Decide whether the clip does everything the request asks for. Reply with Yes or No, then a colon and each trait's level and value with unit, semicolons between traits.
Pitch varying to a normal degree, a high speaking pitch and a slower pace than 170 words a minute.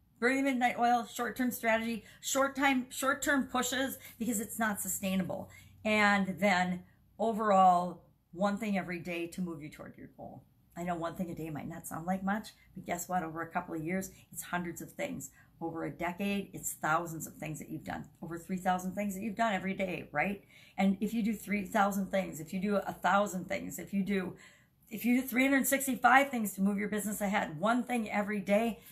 No: average, 4.1 semitones; high, 200 Hz; fast, 205 wpm